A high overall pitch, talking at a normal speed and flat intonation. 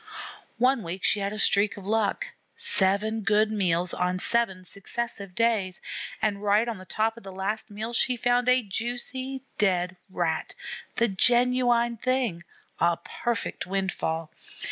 No: high, 210 Hz; average, 145 wpm; average, 3.9 semitones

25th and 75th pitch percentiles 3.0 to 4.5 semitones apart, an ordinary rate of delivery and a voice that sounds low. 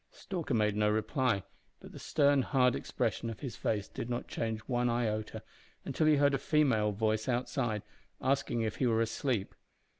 Yes: average, 3.6 semitones; average, 175 wpm; low, 120 Hz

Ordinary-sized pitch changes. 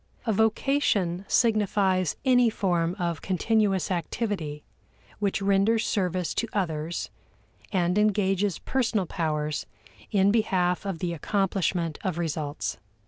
Yes: average, 3.5 semitones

